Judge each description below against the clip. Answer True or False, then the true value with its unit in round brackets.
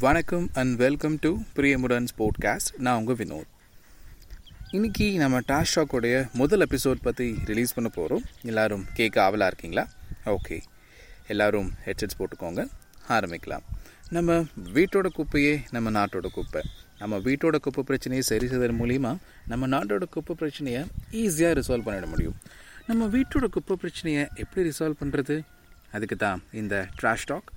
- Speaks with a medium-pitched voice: False (130 Hz)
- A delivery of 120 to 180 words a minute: True (130 wpm)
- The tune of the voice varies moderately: False (6.4 semitones)